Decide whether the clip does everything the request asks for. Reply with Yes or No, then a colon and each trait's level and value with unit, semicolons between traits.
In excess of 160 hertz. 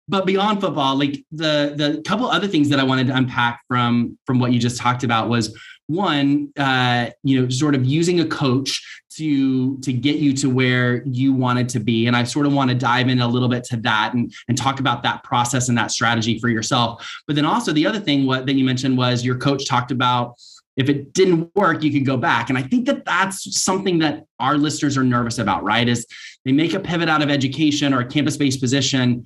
No: low, 135 Hz